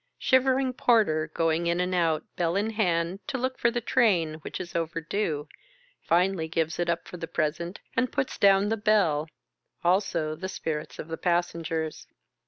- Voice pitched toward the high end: No, medium, 170 Hz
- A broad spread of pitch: No, average, 4.3 semitones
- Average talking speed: Yes, average, 175 wpm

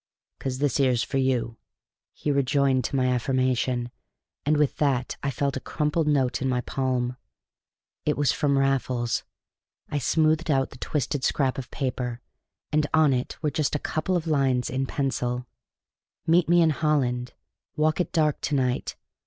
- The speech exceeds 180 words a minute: No, average, 165 wpm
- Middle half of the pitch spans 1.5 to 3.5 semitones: Yes, average, 2.8 semitones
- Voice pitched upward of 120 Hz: Yes, low, 135 Hz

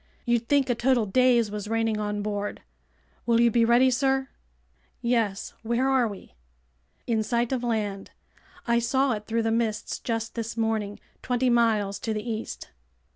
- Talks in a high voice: Yes, high, 230 Hz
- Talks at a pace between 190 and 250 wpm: No, average, 165 wpm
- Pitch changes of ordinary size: No, narrow, 2.1 semitones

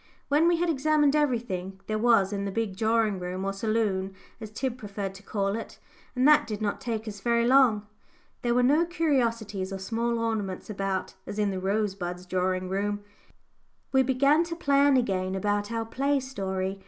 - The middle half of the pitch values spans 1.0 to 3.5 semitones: No, average, 4.7 semitones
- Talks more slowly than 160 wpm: No, average, 180 wpm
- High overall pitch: Yes, high, 215 Hz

